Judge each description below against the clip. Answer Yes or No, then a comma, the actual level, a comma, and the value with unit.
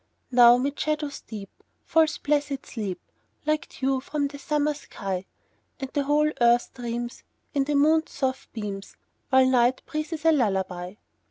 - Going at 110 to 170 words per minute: Yes, average, 150 wpm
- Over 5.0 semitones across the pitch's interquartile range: No, average, 3.9 semitones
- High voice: Yes, very high, 270 Hz